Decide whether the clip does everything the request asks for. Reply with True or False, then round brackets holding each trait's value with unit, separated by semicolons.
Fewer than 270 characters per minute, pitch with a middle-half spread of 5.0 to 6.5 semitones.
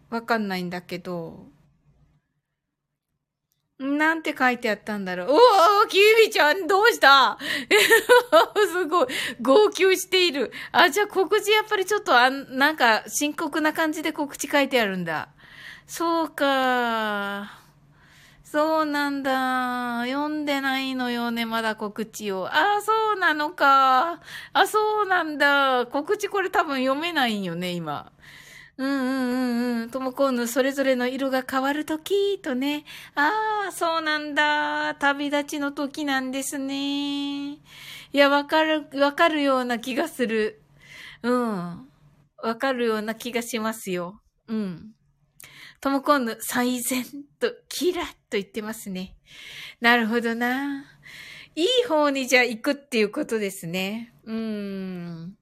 True (260 characters per minute; 5.6 semitones)